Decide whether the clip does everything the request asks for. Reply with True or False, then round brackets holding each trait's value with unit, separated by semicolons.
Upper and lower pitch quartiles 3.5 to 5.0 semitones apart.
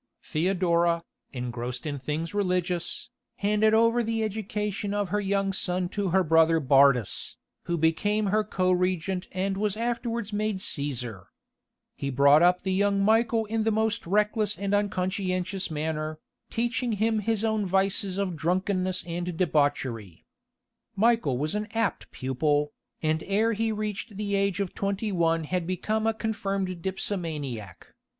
True (4.4 semitones)